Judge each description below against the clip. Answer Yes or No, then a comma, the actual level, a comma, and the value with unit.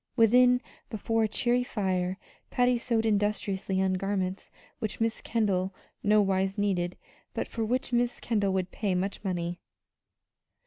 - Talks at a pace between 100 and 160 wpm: Yes, average, 140 wpm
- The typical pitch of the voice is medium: No, high, 205 Hz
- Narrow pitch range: No, average, 3.1 semitones